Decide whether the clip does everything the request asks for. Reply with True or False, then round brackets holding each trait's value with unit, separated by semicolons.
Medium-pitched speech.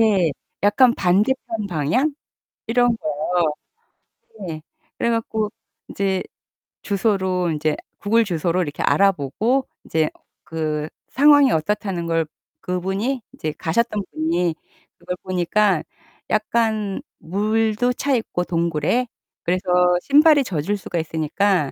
False (195 Hz)